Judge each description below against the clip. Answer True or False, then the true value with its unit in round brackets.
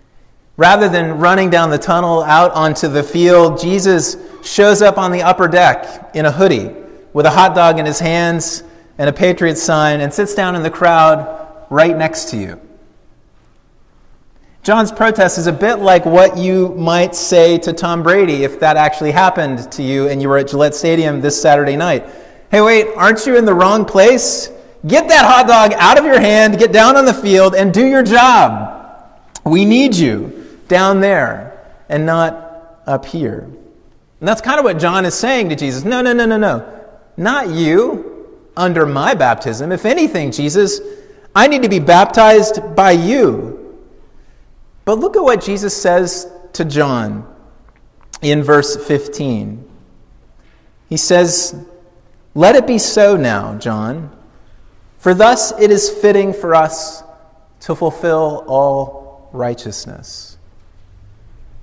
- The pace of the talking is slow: False (160 wpm)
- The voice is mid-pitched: True (175 Hz)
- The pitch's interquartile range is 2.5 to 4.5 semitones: False (5.4 semitones)